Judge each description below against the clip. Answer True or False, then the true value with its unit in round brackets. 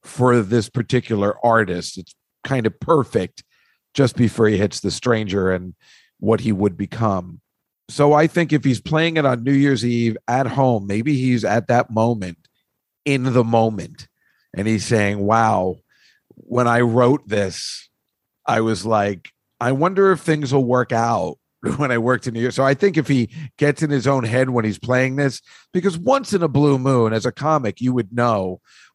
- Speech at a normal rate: True (185 wpm)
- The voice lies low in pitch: True (120 Hz)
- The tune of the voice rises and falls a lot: False (3.9 semitones)